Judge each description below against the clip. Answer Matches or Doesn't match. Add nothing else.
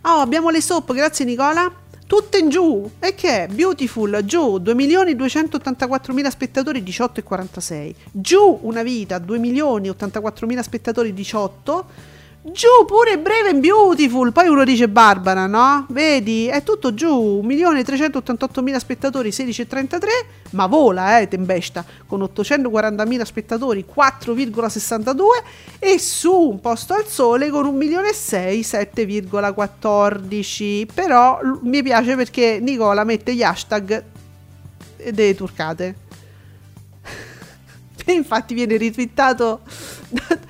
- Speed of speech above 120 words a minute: Doesn't match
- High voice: Matches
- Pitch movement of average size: Doesn't match